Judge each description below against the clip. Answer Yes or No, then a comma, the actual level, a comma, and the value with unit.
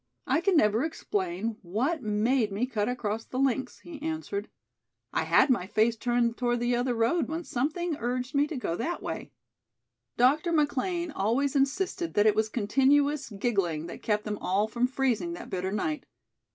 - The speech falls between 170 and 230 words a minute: Yes, average, 175 wpm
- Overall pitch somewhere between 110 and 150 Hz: No, high, 245 Hz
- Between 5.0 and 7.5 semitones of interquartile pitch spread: Yes, wide, 5.4 semitones